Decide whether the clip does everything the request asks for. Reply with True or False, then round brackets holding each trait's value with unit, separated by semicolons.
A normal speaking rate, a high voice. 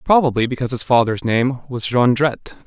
False (155 wpm; 125 Hz)